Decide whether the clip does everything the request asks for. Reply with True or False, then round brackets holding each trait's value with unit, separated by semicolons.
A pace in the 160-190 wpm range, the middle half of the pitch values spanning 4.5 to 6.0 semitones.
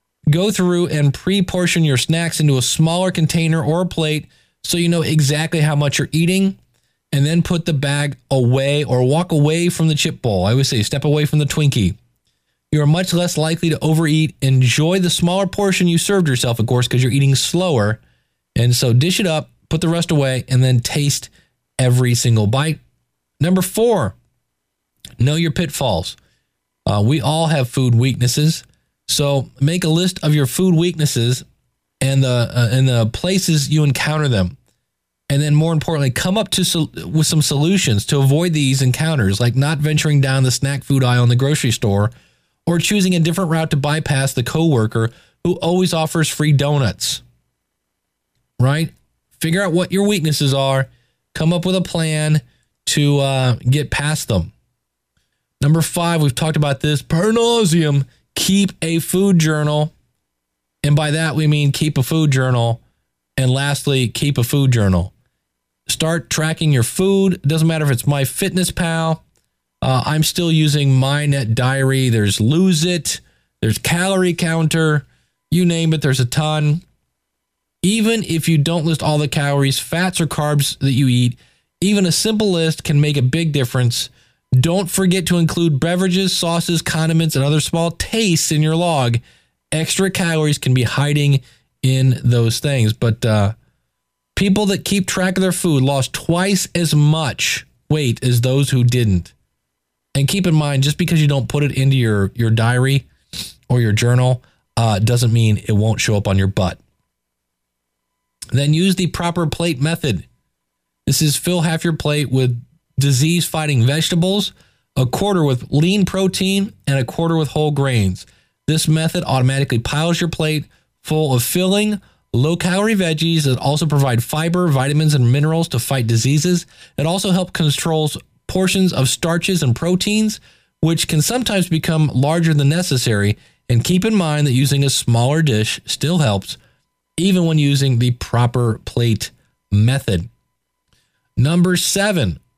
True (165 wpm; 4.9 semitones)